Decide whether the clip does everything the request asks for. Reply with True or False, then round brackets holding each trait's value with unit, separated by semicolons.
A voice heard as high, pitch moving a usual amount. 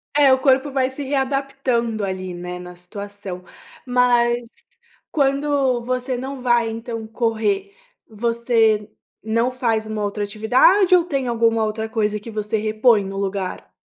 True (230 Hz; 3.5 semitones)